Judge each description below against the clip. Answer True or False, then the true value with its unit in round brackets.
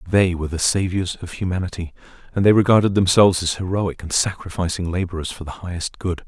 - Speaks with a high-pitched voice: False (90 Hz)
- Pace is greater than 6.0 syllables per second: True (6.2 syllables/s)